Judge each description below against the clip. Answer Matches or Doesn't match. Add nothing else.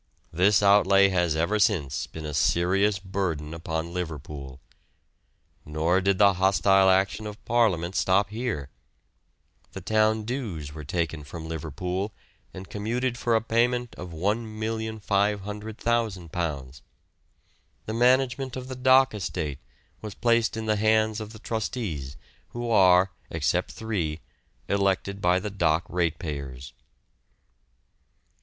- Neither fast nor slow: Doesn't match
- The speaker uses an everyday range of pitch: Matches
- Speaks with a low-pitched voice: Matches